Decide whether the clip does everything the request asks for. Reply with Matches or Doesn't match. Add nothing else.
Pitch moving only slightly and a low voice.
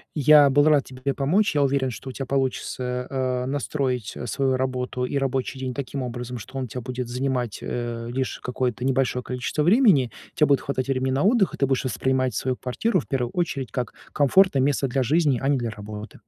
Matches